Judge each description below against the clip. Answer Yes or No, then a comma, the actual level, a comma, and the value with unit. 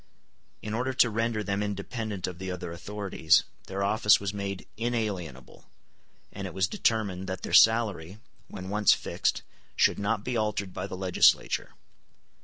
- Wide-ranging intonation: No, average, 2.8 semitones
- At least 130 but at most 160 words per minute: Yes, average, 155 wpm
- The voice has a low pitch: Yes, low, 100 Hz